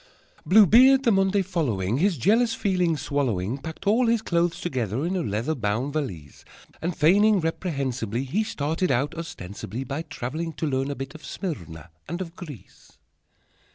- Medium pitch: Yes, medium, 155 Hz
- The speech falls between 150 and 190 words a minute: Yes, average, 160 wpm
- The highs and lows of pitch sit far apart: Yes, wide, 6.4 semitones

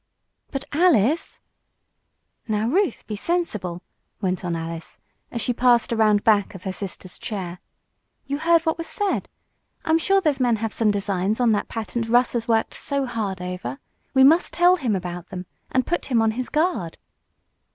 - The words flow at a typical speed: Yes, average, 175 wpm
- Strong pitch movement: Yes, wide, 6.6 semitones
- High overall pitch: Yes, high, 225 Hz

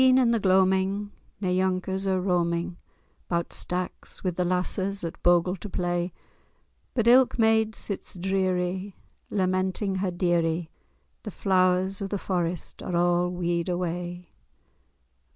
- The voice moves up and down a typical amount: No, narrow, 1.8 semitones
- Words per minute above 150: No, slow, 135 wpm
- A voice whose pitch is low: No, medium, 185 Hz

